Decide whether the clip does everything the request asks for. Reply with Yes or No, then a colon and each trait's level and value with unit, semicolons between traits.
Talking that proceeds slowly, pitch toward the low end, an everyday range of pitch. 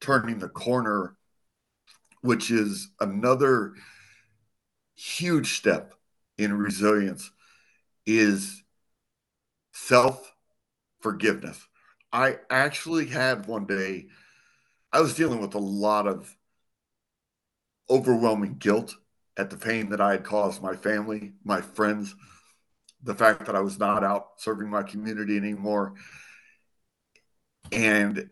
No: slow, 105 wpm; low, 105 Hz; narrow, 2.0 semitones